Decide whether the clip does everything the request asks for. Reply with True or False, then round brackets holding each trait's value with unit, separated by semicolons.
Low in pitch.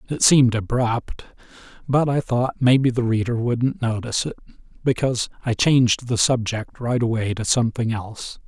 True (120 Hz)